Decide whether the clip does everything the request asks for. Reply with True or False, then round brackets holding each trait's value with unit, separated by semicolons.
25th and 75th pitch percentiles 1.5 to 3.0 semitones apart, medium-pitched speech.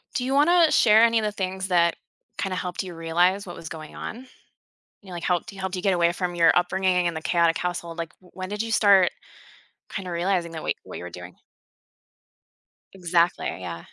True (2.6 semitones; 180 Hz)